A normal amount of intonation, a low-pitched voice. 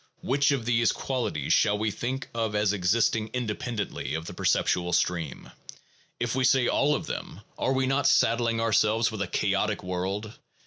Yes: average, 3.5 semitones; low, 115 Hz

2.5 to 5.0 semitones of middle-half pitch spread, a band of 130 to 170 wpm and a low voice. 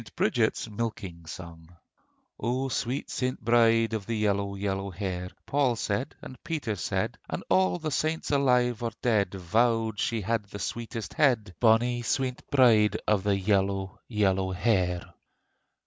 Yes: average, 3.8 semitones; average, 150 wpm; low, 110 Hz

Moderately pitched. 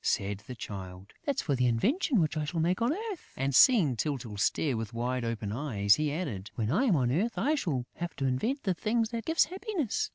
Yes: medium, 150 Hz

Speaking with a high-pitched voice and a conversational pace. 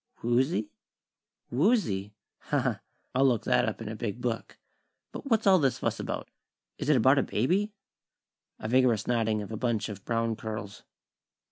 No: low, 120 Hz; average, 165 wpm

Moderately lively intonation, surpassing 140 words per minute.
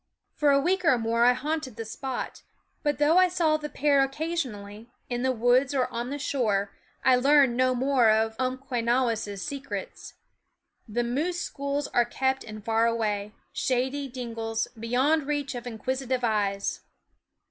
Yes: average, 3.6 semitones; average, 155 wpm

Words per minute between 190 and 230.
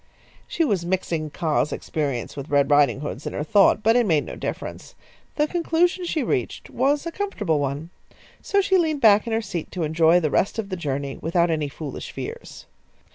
Yes: average, 195 wpm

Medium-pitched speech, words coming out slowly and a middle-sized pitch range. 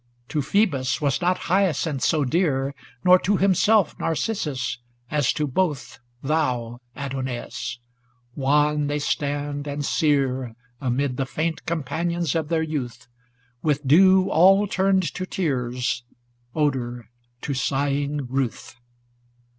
Yes: medium, 145 Hz; slow, 115 wpm; average, 4.0 semitones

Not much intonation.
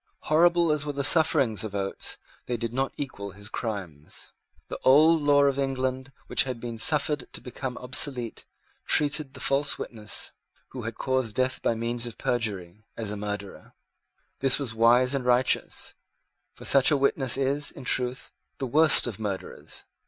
No: average, 3.7 semitones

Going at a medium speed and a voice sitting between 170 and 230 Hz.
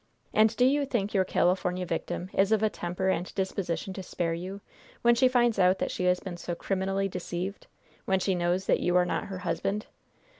No: fast, 210 wpm; high, 190 Hz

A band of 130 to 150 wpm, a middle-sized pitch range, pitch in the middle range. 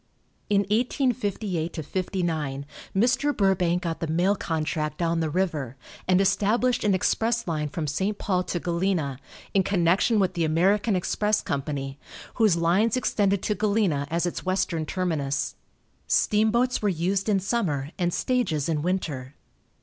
Yes: average, 140 wpm; average, 4.3 semitones; medium, 180 Hz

